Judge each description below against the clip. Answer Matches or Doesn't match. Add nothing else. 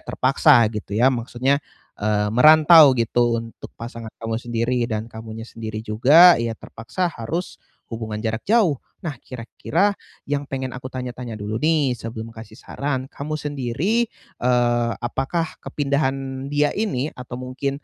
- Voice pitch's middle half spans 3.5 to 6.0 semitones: Matches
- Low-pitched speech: Matches